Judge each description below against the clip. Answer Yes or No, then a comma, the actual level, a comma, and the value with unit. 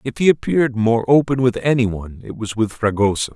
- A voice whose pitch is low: Yes, low, 120 Hz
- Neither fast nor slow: No, fast, 215 wpm